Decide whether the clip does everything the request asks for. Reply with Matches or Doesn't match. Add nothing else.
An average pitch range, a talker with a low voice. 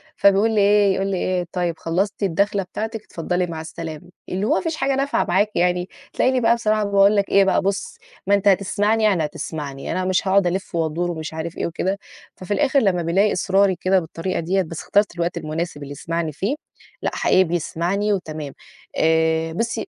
Doesn't match